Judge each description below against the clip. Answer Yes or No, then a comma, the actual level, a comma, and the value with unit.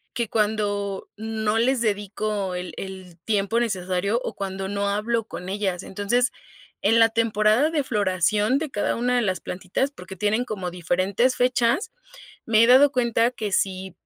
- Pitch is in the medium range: No, high, 210 Hz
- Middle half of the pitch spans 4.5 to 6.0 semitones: No, average, 3.5 semitones